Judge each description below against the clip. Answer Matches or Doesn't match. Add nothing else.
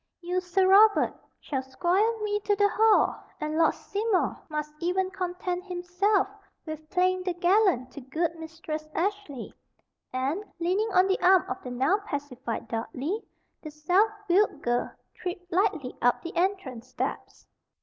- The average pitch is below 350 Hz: Doesn't match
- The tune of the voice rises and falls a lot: Doesn't match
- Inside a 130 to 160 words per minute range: Matches